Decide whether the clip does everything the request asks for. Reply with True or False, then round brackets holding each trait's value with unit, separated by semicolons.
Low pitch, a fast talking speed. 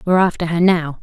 False (170 Hz; 235 wpm)